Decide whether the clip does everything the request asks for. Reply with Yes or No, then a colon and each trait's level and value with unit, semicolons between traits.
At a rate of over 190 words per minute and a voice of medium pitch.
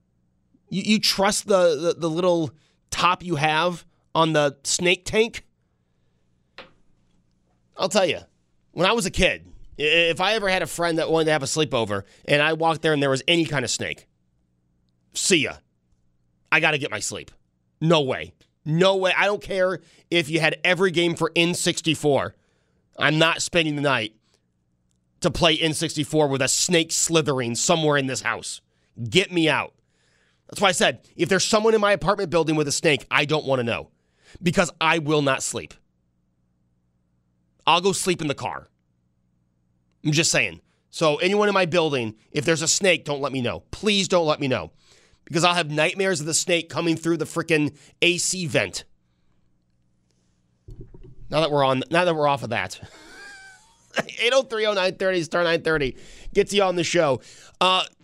No: average, 175 wpm; medium, 150 Hz